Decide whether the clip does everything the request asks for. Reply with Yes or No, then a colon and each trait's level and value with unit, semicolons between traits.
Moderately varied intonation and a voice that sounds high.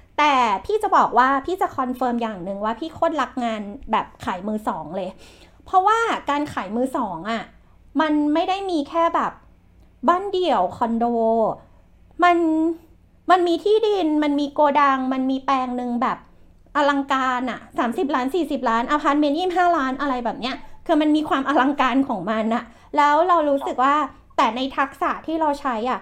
Yes: average, 4.8 semitones; very high, 285 Hz